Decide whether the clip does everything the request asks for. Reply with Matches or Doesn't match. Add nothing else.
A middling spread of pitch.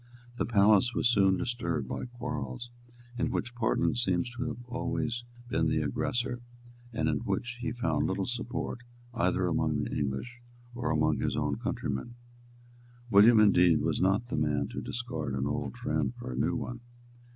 Doesn't match